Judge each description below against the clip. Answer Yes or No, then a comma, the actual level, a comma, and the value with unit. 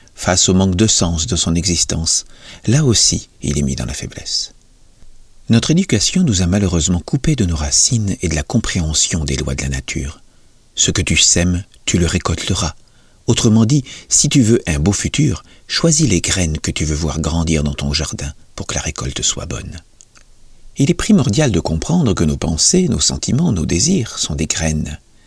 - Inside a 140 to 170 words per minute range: No, average, 195 wpm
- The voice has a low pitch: Yes, very low, 85 Hz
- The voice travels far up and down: Yes, wide, 5.9 semitones